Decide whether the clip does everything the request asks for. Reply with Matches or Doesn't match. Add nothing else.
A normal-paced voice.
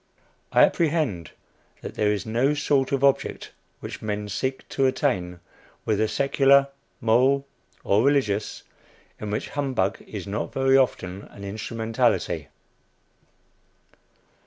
Doesn't match